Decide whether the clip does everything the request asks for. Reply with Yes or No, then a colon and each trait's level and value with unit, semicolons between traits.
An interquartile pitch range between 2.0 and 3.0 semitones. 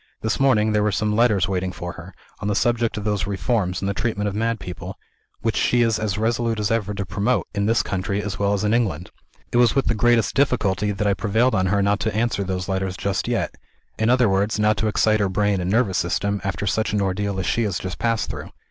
Yes: narrow, 2.6 semitones